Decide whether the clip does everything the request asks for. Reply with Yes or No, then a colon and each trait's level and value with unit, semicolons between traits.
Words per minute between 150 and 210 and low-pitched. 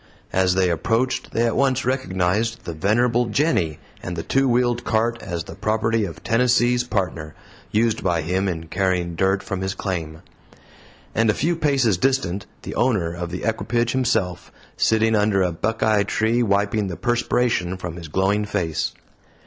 Yes: average, 165 wpm; low, 105 Hz